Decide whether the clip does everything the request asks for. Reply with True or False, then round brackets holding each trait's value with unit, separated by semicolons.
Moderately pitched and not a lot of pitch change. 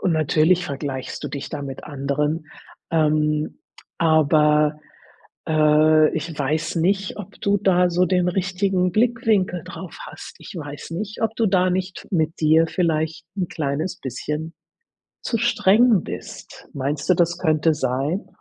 False (160 Hz; 3.4 semitones)